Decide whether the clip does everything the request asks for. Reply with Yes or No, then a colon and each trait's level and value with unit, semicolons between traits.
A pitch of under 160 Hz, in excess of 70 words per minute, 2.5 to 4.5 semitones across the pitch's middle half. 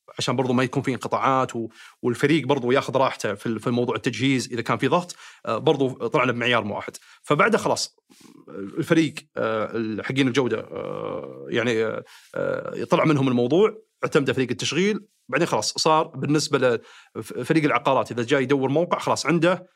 No: medium, 140 Hz; fast, 135 wpm; average, 5.3 semitones